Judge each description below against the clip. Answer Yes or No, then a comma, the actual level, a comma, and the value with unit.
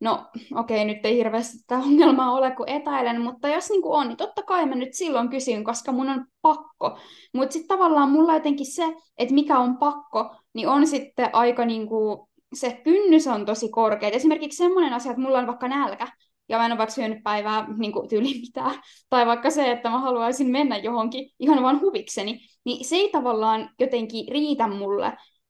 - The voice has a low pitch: No, very high, 260 Hz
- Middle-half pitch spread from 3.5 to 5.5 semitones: Yes, average, 4.2 semitones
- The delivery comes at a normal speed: No, fast, 200 wpm